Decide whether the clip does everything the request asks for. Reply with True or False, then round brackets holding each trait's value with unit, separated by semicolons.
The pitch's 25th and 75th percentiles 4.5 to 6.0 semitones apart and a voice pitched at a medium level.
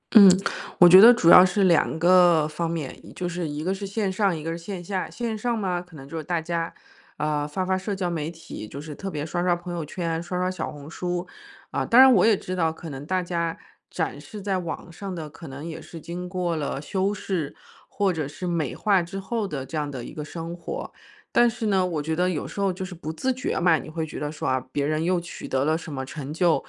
False (3.2 semitones; 175 Hz)